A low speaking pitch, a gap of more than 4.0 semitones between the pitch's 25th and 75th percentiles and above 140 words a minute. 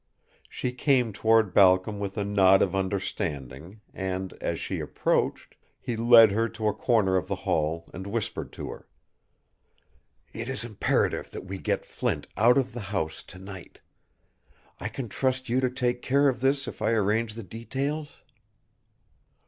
Yes: low, 110 Hz; average, 4.4 semitones; average, 165 wpm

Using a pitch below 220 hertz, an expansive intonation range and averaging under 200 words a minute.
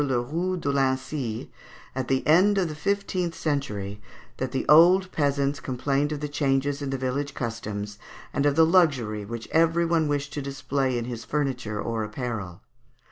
No: medium, 140 Hz; average, 3.9 semitones; average, 175 wpm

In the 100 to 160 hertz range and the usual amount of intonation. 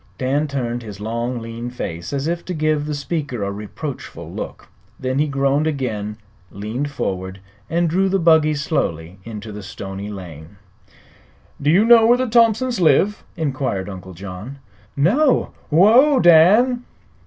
No: medium, 140 Hz; wide, 8.5 semitones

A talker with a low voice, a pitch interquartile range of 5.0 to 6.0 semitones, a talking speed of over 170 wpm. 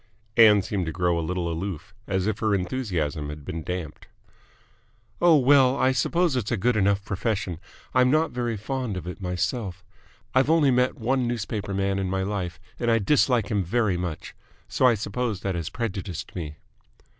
Yes: low, 100 Hz; wide, 5.4 semitones; average, 180 wpm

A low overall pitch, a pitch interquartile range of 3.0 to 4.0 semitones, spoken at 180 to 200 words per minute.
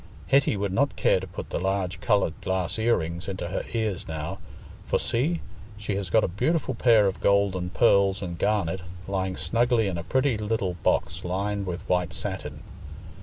Yes: very low, 95 Hz; average, 3.3 semitones; average, 185 wpm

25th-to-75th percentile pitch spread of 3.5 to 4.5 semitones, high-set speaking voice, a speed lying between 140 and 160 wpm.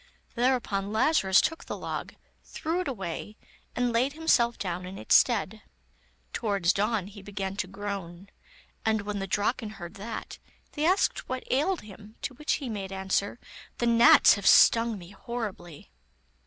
Yes: average, 4.0 semitones; high, 210 Hz; average, 155 wpm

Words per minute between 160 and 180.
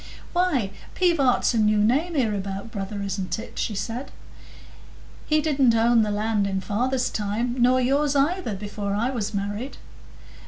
No: average, 150 wpm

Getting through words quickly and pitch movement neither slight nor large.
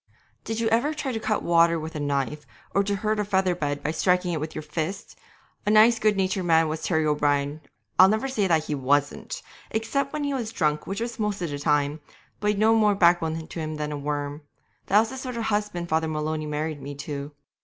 No: fast, 240 wpm; wide, 5.9 semitones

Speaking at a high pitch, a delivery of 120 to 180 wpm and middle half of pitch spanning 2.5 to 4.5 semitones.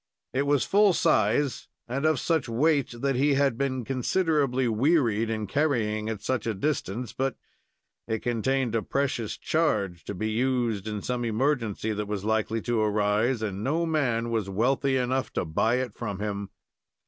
No: low, 120 Hz; average, 170 wpm; average, 4.1 semitones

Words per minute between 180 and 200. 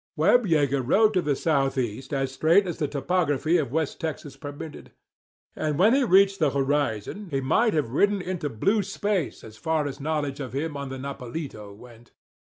Yes: average, 190 wpm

